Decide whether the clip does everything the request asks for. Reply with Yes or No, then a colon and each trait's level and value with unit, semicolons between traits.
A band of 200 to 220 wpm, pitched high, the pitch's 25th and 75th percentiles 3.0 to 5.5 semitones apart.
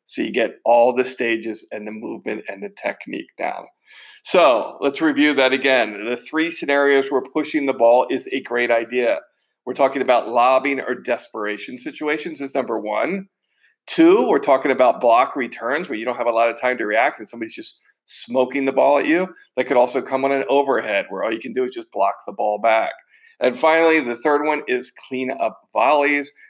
No: fast, 205 wpm; low, 135 Hz; average, 3.7 semitones